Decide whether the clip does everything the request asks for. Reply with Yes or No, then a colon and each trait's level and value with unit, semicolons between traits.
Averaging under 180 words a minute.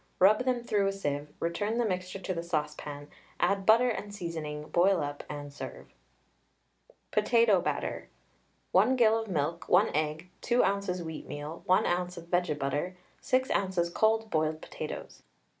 Yes: average, 155 wpm